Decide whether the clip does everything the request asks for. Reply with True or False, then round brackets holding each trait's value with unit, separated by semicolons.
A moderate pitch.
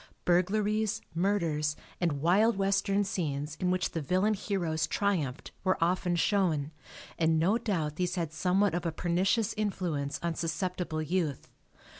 True (180 Hz)